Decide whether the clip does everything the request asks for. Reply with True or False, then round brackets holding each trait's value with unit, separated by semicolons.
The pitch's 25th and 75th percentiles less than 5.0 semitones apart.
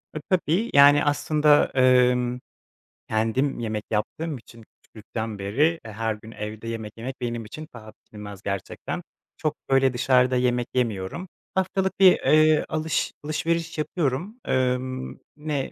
False (5.4 semitones)